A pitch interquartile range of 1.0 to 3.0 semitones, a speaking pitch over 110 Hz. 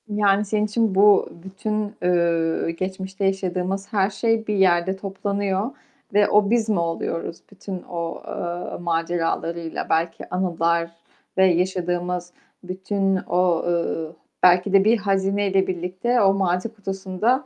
Yes: narrow, 2.6 semitones; high, 190 Hz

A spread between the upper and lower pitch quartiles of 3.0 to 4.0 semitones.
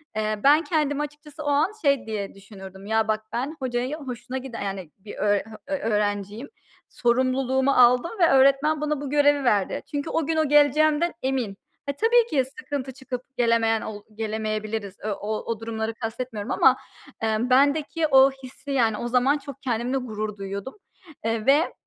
No: average, 4.7 semitones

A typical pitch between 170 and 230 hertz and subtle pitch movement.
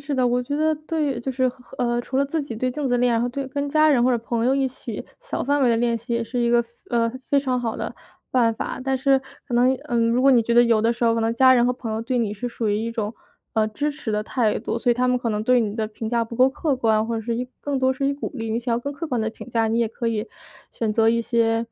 No: high, 240 Hz; narrow, 2.3 semitones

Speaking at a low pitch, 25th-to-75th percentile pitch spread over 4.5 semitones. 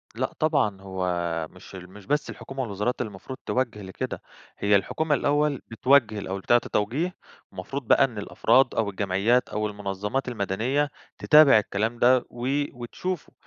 Yes: low, 115 Hz; average, 5.0 semitones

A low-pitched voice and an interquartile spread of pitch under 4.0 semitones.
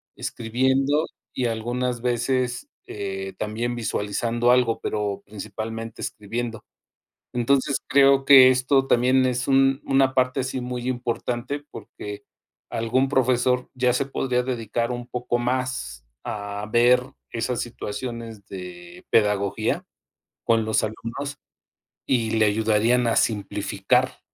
Yes: low, 120 Hz; narrow, 2.5 semitones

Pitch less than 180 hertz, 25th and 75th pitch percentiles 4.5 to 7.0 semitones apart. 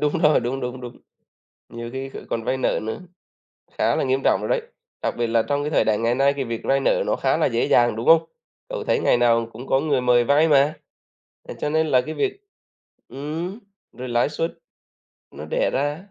No: low, 135 Hz; average, 4.0 semitones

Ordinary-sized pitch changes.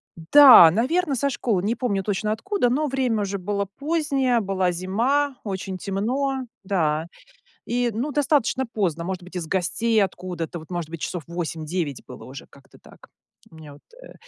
No: wide, 6.7 semitones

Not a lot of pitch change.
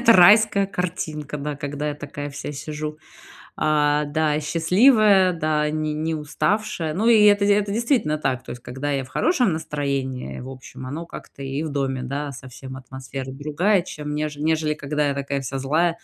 No: average, 3.5 semitones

